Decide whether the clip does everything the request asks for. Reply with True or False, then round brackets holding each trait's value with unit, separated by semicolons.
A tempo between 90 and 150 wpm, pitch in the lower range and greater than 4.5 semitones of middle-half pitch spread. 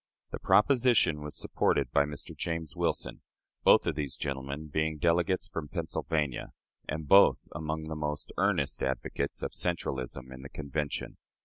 False (145 wpm; 75 Hz; 2.7 semitones)